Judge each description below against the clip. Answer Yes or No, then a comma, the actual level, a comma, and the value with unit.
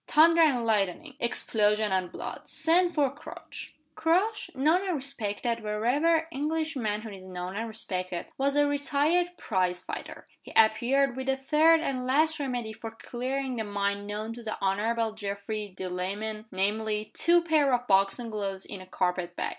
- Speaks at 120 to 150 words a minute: No, average, 160 wpm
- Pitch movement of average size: No, wide, 5.9 semitones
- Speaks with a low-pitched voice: No, high, 230 Hz